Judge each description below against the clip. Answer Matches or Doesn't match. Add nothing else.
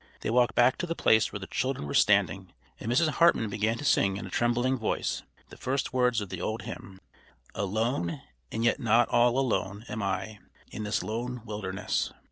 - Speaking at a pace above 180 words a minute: Matches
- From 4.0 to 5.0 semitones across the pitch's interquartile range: Doesn't match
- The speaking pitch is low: Matches